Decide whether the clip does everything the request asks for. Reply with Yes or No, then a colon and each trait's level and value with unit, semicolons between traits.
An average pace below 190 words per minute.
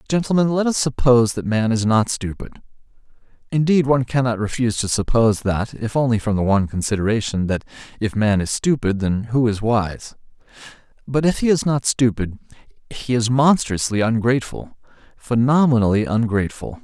Yes: average, 155 wpm